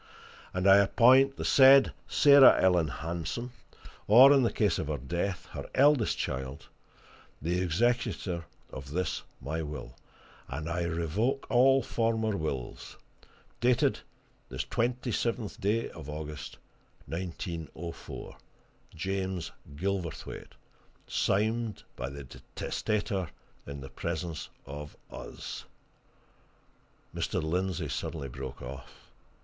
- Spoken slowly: Yes, slow, 110 wpm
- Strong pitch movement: Yes, wide, 7.0 semitones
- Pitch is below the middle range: Yes, very low, 90 Hz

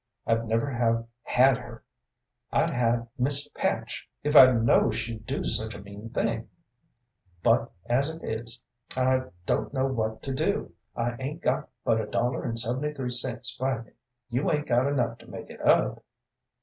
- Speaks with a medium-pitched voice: No, low, 120 Hz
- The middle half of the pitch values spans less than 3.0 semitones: Yes, narrow, 2.4 semitones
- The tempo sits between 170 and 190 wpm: Yes, average, 175 wpm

